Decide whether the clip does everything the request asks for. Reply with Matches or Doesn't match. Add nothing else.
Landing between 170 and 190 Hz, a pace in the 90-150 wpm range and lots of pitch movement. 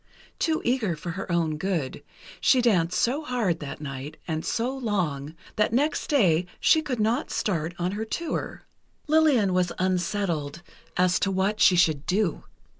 Doesn't match